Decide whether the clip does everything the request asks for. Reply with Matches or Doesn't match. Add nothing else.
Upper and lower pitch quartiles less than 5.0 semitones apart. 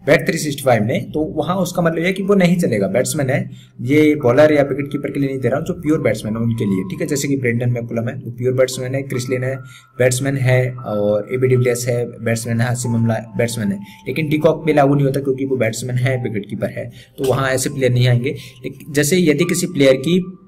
Matches